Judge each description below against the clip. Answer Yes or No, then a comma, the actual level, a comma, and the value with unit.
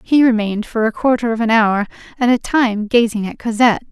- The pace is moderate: No, fast, 215 wpm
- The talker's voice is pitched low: No, high, 230 Hz